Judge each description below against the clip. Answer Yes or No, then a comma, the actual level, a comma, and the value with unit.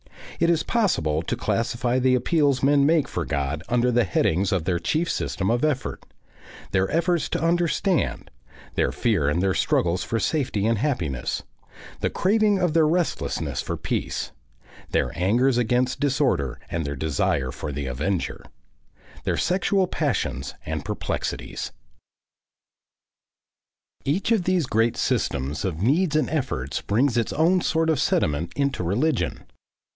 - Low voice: Yes, low, 120 Hz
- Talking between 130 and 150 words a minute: Yes, average, 145 wpm